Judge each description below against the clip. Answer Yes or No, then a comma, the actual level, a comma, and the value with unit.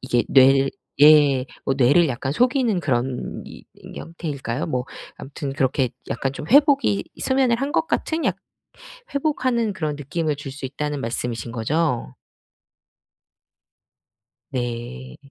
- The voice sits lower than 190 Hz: Yes, medium, 140 Hz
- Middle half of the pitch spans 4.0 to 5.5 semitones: Yes, average, 5.2 semitones